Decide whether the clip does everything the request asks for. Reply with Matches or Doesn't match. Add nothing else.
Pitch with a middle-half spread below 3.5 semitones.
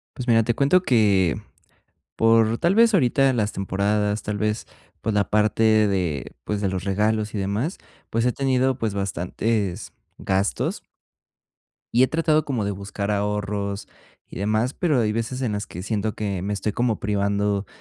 Matches